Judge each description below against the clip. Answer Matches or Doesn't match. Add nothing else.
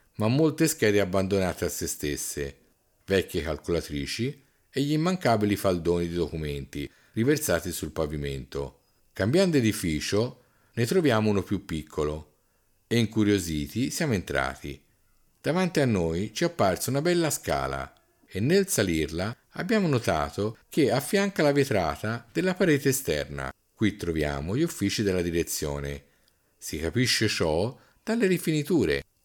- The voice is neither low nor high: Doesn't match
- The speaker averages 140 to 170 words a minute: Doesn't match